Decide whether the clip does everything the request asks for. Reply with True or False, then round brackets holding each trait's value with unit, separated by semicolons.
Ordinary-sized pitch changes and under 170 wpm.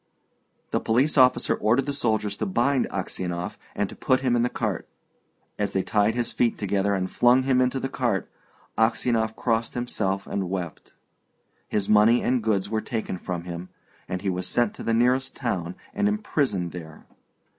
False (4.4 semitones; 175 wpm)